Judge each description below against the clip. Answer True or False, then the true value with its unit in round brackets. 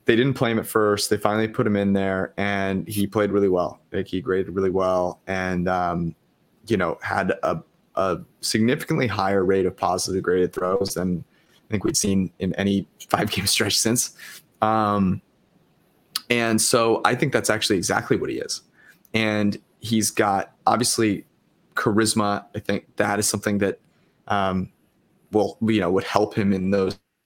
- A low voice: True (100 Hz)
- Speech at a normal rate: True (170 wpm)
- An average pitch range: False (2.3 semitones)